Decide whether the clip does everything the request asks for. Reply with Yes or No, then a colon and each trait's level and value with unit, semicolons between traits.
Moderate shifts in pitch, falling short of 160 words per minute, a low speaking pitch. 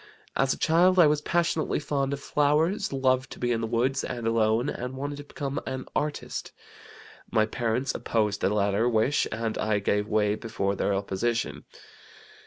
No: average, 4.7 semitones; average, 175 wpm; low, 120 Hz